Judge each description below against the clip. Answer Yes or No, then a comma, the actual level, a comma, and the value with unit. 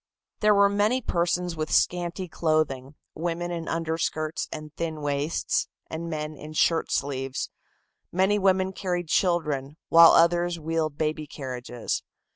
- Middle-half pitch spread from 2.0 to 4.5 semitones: Yes, narrow, 2.5 semitones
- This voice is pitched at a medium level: Yes, medium, 165 Hz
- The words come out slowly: Yes, slow, 130 wpm